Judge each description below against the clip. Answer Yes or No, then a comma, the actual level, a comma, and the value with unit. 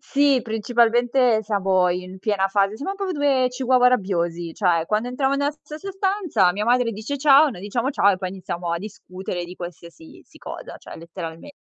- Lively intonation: Yes, wide, 6.6 semitones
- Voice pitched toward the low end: No, high, 215 Hz